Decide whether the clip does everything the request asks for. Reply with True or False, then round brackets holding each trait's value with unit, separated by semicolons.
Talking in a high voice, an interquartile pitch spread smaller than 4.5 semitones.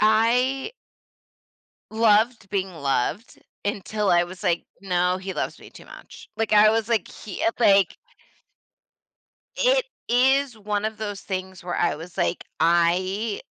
True (205 Hz; 3.6 semitones)